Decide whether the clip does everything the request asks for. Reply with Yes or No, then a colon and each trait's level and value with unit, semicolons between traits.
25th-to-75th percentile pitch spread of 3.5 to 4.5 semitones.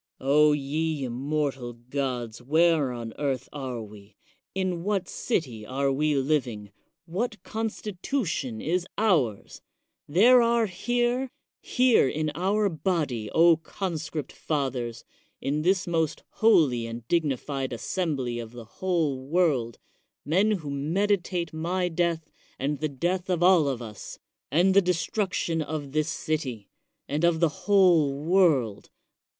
No: wide, 5.5 semitones